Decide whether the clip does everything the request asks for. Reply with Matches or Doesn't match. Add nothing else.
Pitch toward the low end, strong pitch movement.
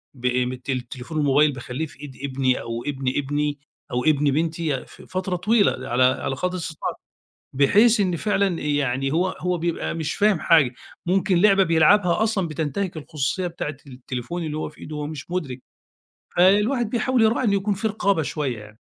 Doesn't match